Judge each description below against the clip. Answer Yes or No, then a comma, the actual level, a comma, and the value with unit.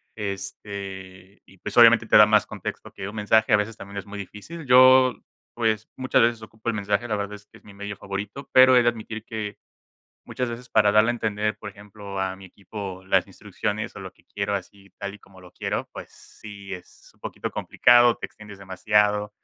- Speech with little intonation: Yes, narrow, 2.2 semitones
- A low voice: Yes, low, 105 Hz